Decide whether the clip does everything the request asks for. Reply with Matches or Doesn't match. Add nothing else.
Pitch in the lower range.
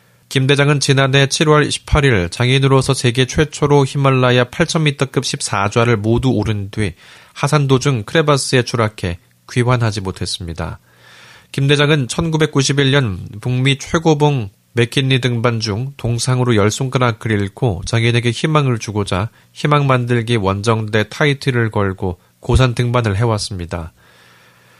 Matches